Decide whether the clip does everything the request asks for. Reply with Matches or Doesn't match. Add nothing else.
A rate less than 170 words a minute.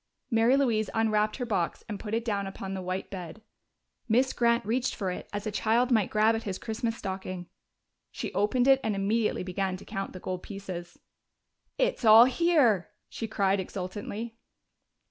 Doesn't match